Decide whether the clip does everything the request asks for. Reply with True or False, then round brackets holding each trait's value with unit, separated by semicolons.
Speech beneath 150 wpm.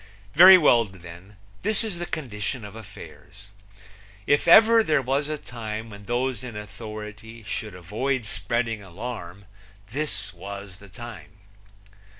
True (135 wpm)